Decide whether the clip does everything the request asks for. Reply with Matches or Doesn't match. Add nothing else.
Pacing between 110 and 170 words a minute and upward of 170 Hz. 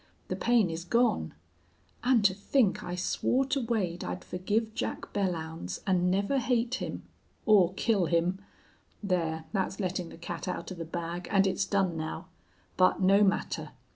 Matches